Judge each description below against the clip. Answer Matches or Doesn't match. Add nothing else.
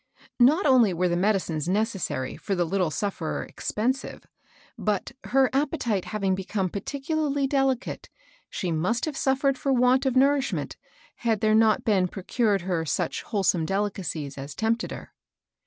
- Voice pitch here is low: Doesn't match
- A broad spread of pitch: Matches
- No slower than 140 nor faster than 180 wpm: Matches